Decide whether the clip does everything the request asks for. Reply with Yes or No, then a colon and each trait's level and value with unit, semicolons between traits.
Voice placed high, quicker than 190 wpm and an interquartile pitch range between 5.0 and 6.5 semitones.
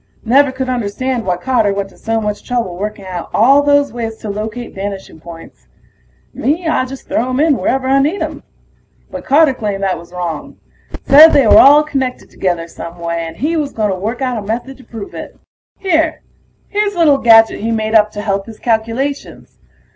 Yes: high, 230 Hz; average, 200 wpm; average, 5.3 semitones